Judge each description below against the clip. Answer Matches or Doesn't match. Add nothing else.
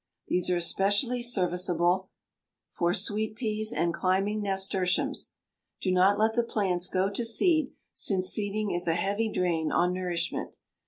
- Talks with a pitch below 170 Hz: Doesn't match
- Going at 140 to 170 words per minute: Matches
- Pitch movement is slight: Doesn't match